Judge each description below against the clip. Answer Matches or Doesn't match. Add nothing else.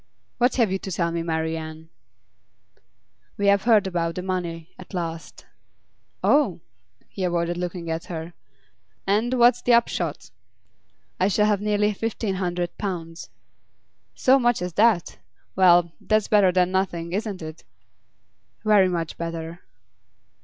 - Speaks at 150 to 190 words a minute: Doesn't match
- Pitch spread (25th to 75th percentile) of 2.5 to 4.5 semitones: Matches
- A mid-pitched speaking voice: Matches